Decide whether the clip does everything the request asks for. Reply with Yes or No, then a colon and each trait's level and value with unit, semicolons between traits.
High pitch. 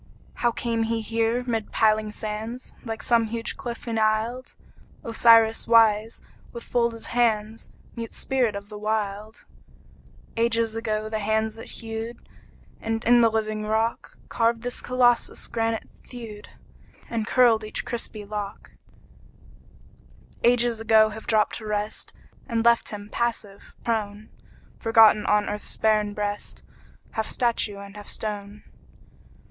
Yes: high, 225 Hz